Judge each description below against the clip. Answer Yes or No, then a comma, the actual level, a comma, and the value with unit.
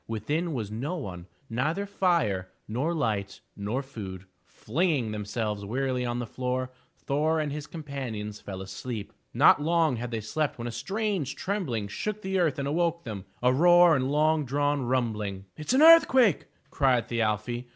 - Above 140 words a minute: Yes, average, 170 wpm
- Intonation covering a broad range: Yes, wide, 6.5 semitones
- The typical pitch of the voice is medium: No, low, 130 Hz